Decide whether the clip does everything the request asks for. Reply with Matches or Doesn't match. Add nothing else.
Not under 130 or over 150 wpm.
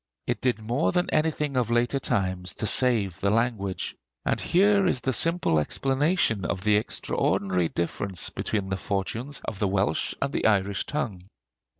Doesn't match